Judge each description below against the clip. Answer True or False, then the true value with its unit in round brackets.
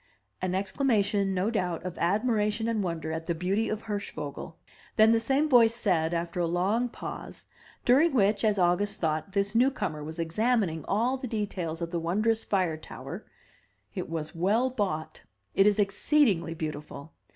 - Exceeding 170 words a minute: False (165 wpm)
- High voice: True (195 Hz)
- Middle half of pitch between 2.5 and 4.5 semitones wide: False (5.0 semitones)